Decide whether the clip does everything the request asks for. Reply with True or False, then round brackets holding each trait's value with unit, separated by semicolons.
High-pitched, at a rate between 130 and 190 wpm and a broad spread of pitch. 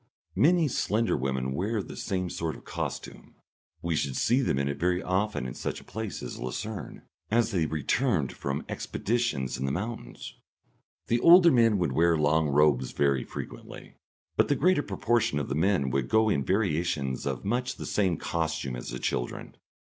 False (85 Hz; 175 wpm; 8.3 semitones)